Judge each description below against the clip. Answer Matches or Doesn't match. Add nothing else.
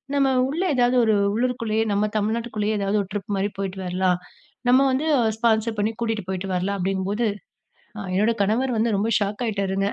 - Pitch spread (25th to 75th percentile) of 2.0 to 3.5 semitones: Matches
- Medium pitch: Doesn't match